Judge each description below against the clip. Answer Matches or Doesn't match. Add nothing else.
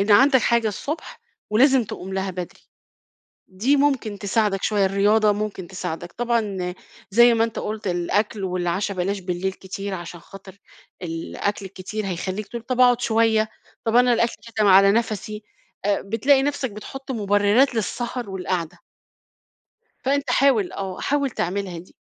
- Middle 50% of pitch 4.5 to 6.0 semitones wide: Doesn't match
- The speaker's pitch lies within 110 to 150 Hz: Doesn't match